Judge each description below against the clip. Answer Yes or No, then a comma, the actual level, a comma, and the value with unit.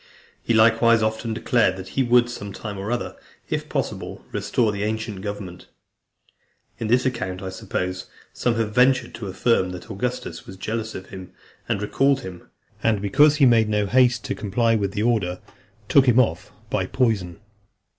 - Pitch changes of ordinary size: Yes, average, 3.6 semitones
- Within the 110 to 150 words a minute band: No, average, 175 wpm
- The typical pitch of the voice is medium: No, low, 110 Hz